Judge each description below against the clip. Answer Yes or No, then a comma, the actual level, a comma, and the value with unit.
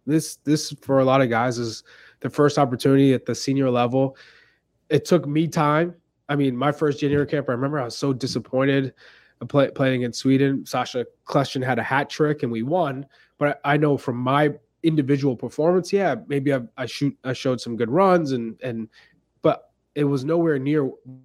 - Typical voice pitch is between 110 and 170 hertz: Yes, medium, 140 Hz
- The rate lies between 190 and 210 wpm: Yes, average, 195 wpm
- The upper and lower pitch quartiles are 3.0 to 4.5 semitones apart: No, narrow, 2.5 semitones